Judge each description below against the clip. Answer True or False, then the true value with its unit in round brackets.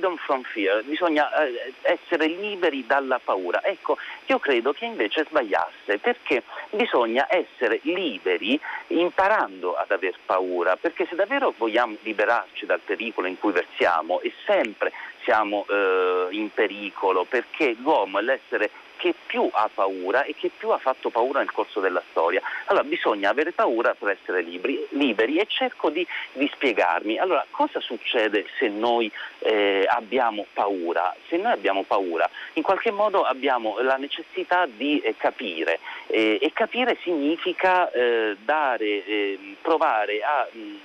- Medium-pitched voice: True (165 Hz)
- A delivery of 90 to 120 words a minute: False (145 wpm)